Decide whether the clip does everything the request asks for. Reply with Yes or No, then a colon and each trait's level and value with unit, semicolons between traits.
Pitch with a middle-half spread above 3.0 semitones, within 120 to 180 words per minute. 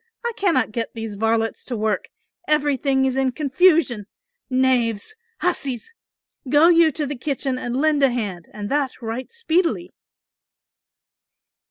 Yes: average, 5.0 semitones; slow, 135 wpm